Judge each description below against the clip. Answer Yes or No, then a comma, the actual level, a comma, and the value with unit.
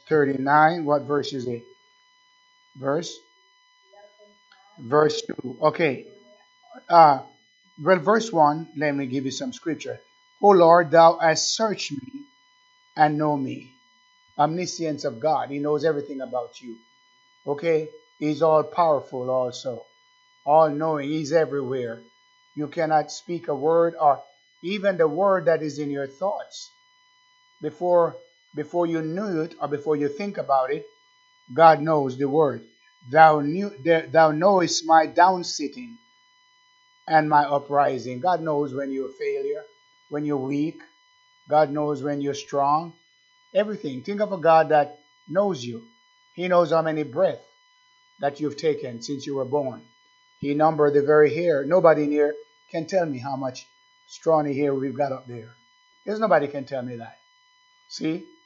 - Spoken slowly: No, average, 150 wpm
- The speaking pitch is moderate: Yes, medium, 165 Hz